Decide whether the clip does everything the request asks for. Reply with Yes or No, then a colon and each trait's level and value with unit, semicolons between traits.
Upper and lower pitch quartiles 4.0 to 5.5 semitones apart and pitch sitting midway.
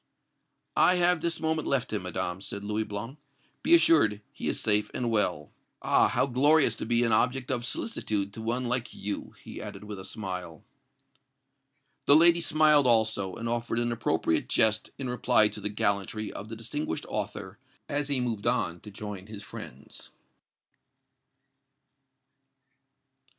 No: average, 4.4 semitones; low, 115 Hz